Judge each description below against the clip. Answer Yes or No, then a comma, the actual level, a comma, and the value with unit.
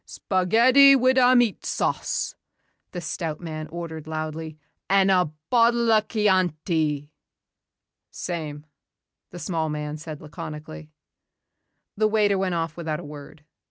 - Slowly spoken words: Yes, slow, 125 wpm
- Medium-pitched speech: Yes, medium, 170 Hz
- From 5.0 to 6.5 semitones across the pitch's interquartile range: Yes, average, 5.3 semitones